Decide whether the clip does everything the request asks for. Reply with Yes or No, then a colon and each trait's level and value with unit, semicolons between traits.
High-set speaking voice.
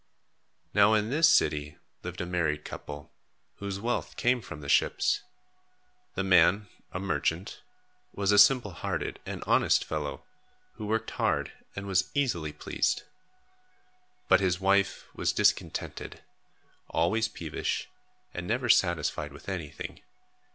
No: very low, 95 Hz